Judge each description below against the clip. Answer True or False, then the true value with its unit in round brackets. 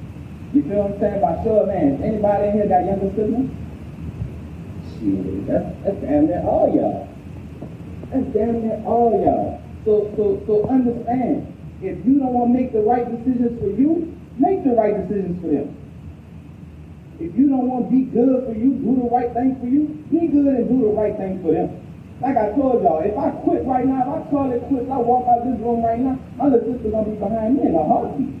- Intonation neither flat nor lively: True (3.5 semitones)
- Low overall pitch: False (240 Hz)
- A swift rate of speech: True (210 wpm)